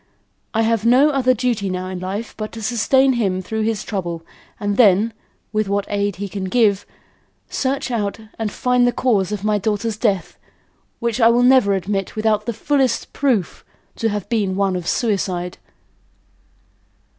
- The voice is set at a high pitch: Yes, high, 215 Hz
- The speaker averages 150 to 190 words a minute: Yes, average, 170 wpm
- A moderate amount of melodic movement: Yes, average, 3.3 semitones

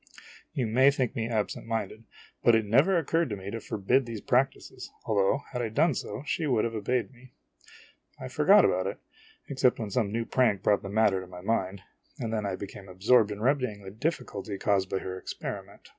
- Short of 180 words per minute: No, fast, 205 wpm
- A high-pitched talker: No, low, 115 Hz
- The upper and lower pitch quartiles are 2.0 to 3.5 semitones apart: No, average, 4.3 semitones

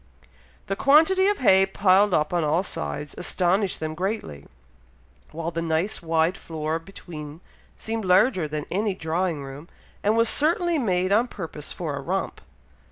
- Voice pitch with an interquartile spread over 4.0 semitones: Yes, average, 4.5 semitones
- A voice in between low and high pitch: Yes, medium, 180 Hz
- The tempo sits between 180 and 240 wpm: No, average, 155 wpm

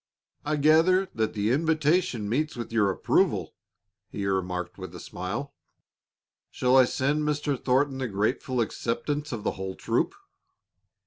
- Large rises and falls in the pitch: Yes, wide, 6.5 semitones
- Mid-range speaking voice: No, low, 125 Hz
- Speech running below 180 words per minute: Yes, average, 140 wpm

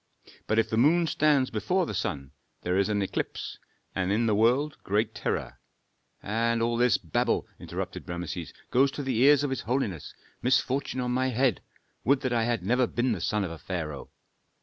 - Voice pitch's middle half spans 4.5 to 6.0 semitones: Yes, average, 4.8 semitones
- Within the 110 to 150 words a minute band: No, average, 195 wpm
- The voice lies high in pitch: No, low, 115 Hz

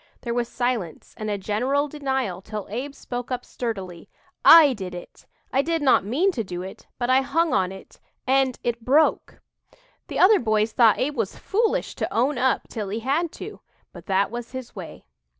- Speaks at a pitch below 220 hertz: No, high, 245 Hz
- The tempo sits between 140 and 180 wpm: No, average, 190 wpm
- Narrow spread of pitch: No, average, 4.6 semitones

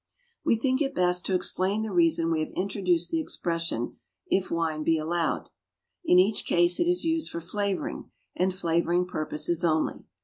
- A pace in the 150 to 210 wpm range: Yes, average, 170 wpm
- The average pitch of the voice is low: No, medium, 180 Hz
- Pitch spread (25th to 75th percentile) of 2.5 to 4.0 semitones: Yes, average, 3.2 semitones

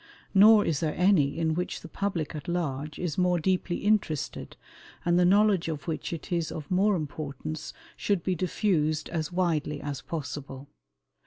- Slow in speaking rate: No, average, 165 wpm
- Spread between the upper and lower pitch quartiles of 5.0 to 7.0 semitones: No, average, 3.4 semitones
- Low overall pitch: No, medium, 165 Hz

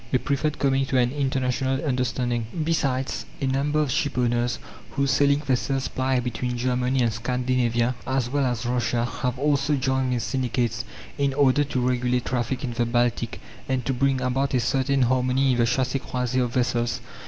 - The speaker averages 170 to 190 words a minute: Yes, average, 175 wpm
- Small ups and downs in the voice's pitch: Yes, narrow, 1.7 semitones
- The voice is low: Yes, low, 130 Hz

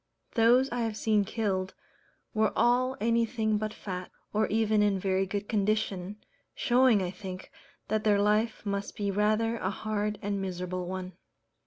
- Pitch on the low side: No, high, 210 Hz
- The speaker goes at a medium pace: Yes, average, 155 wpm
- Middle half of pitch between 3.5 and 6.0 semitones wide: No, narrow, 2.4 semitones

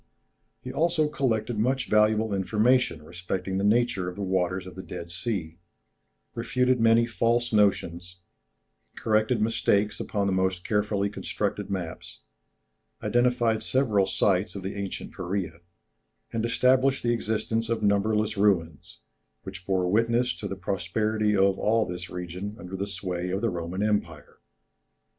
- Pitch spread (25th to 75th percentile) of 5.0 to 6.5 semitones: No, average, 3.6 semitones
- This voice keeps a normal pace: Yes, average, 145 wpm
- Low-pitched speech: Yes, low, 105 Hz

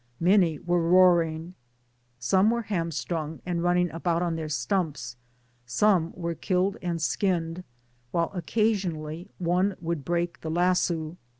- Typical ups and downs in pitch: No, narrow, 2.1 semitones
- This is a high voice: No, medium, 170 Hz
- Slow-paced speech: Yes, slow, 130 wpm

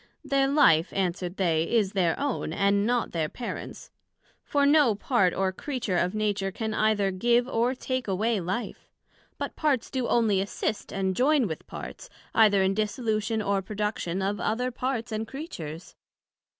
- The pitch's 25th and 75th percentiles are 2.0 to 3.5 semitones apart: No, average, 4.3 semitones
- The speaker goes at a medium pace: Yes, average, 160 wpm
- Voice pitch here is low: No, high, 215 Hz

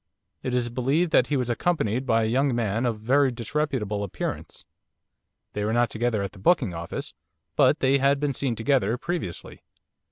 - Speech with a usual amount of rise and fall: Yes, average, 3.9 semitones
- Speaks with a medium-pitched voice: No, low, 120 Hz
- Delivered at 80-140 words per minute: No, average, 180 wpm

